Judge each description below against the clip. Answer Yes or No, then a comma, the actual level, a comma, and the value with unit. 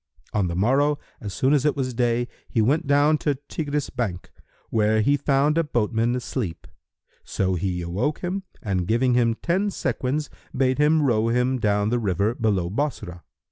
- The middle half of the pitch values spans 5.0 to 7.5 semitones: Yes, average, 5.3 semitones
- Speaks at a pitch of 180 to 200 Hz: No, low, 120 Hz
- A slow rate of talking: No, average, 175 wpm